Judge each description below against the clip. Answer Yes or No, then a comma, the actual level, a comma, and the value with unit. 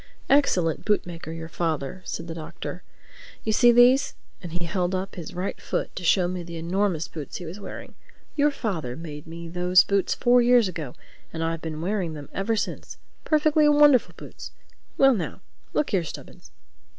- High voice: No, medium, 180 Hz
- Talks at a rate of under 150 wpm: No, average, 170 wpm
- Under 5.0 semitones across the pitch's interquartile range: No, wide, 5.4 semitones